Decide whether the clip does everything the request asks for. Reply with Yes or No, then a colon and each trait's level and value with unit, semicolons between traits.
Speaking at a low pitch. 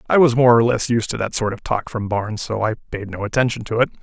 Yes: low, 115 Hz